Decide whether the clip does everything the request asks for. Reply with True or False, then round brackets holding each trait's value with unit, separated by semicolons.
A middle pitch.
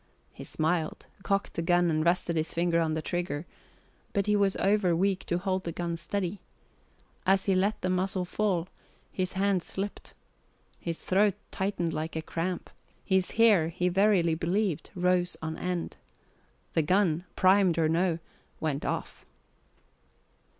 True (180 Hz)